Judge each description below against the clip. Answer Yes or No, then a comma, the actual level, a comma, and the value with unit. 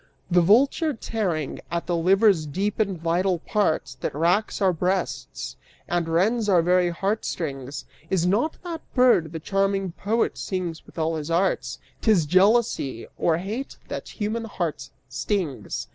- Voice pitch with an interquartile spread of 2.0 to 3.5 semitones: No, average, 4.1 semitones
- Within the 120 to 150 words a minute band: Yes, average, 145 wpm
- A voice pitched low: No, medium, 185 Hz